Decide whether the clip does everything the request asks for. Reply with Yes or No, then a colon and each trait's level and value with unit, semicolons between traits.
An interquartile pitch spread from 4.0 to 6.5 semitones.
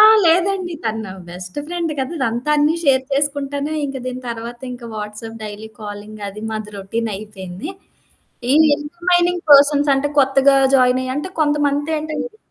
Yes: average, 5.1 semitones